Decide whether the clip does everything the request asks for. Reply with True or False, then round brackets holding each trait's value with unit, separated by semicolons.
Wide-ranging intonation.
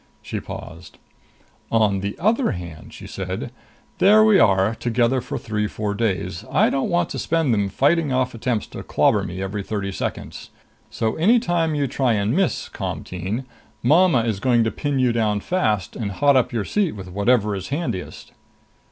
True (6.3 semitones)